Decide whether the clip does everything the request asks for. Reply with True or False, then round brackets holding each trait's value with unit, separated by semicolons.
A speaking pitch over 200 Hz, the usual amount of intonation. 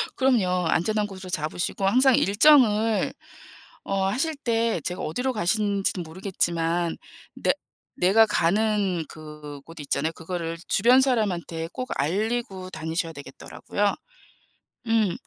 False (195 Hz; 5.0 semitones)